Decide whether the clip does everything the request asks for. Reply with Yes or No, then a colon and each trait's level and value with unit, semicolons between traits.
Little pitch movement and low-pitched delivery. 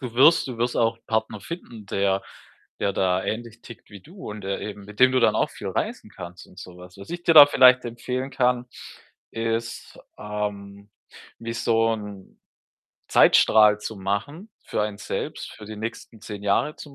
No: average, 3.5 semitones; low, 110 Hz